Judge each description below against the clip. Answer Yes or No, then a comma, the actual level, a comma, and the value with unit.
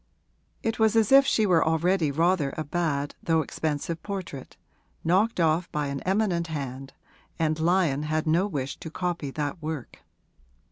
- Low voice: No, medium, 160 Hz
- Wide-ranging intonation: No, average, 3.7 semitones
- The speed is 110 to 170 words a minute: Yes, average, 155 wpm